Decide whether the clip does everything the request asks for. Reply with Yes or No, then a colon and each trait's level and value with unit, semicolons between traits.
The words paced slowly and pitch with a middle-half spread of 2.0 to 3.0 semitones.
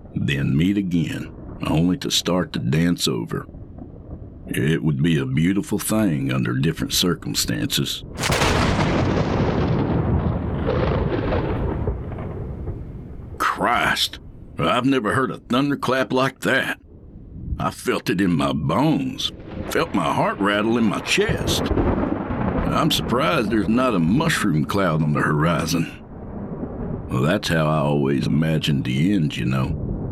No: slow, 120 wpm; average, 5.3 semitones